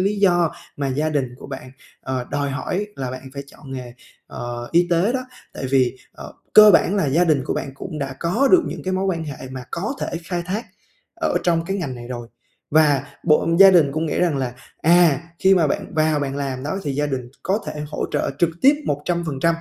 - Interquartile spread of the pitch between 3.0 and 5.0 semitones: Yes, average, 4.7 semitones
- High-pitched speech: No, medium, 150 Hz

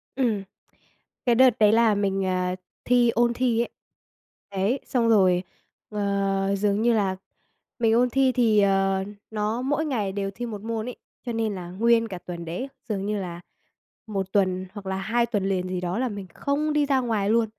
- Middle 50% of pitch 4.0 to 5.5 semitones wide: No, average, 3.5 semitones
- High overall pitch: Yes, high, 210 Hz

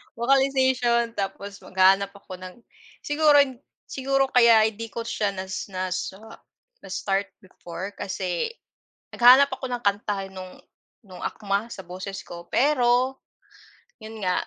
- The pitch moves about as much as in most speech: Yes, average, 4.4 semitones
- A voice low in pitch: No, high, 210 Hz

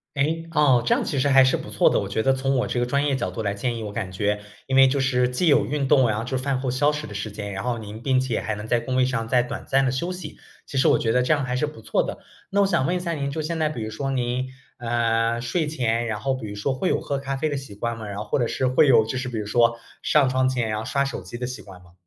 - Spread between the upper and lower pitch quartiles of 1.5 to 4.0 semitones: Yes, average, 3.3 semitones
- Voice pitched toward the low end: Yes, low, 125 Hz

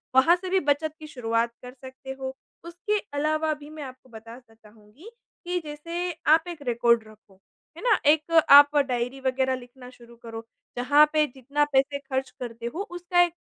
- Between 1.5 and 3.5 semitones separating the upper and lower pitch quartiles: No, average, 4.1 semitones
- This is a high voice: Yes, very high, 270 Hz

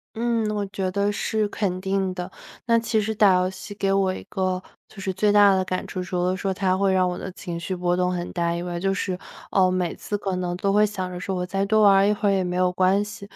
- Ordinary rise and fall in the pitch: No, narrow, 1.9 semitones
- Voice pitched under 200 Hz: Yes, high, 190 Hz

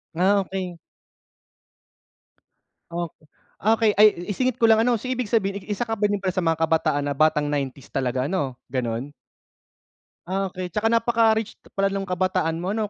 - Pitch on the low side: No, high, 190 Hz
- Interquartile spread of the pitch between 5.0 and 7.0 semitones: Yes, wide, 5.4 semitones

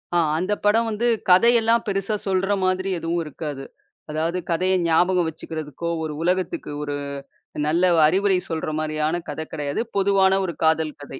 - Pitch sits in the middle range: Yes, medium, 175 Hz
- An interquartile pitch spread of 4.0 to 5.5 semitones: No, average, 3.6 semitones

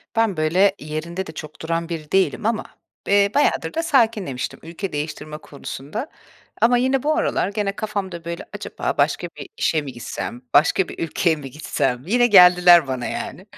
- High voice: No, medium, 175 Hz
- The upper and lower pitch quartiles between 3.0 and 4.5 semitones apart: No, average, 5.3 semitones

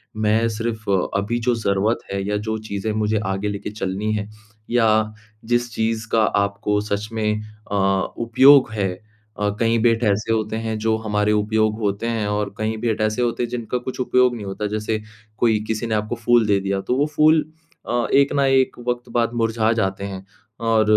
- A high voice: No, low, 110 Hz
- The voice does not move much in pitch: Yes, narrow, 2.0 semitones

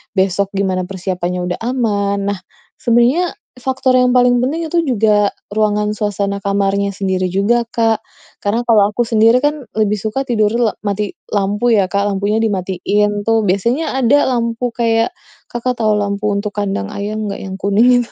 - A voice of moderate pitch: No, high, 210 Hz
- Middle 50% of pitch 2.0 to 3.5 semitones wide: Yes, average, 3.1 semitones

